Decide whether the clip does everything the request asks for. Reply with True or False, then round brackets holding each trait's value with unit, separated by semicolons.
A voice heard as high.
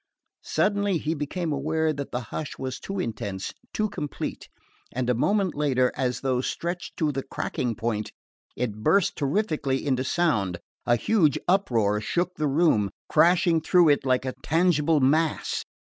False (145 Hz)